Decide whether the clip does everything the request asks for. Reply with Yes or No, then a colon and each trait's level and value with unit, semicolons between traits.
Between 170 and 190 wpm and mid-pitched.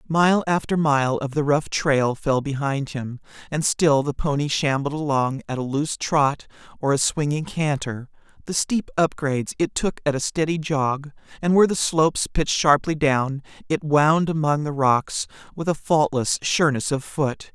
Yes: average, 175 wpm; medium, 145 Hz